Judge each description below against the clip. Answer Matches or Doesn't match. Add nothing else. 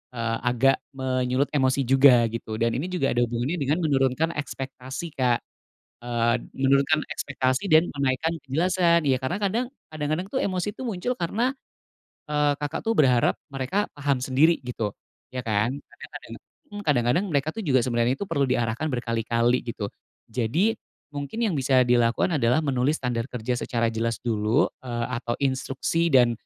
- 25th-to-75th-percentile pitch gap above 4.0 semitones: Matches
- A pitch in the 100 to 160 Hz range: Matches